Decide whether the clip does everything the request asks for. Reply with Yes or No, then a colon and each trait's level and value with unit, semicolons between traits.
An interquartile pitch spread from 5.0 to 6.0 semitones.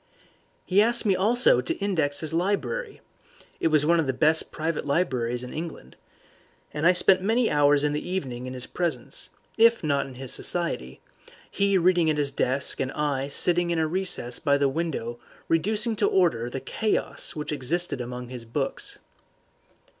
Yes: wide, 5.5 semitones